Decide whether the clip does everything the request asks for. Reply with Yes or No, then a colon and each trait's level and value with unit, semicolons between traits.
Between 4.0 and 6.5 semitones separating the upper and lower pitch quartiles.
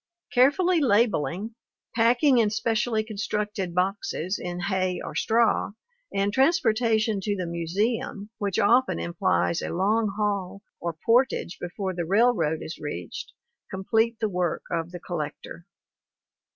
Yes: average, 4.3 semitones